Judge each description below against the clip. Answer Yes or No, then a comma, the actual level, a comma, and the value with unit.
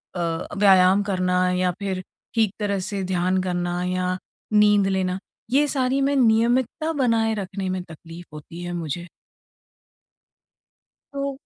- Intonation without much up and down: No, average, 3.5 semitones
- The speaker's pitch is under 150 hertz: No, high, 190 Hz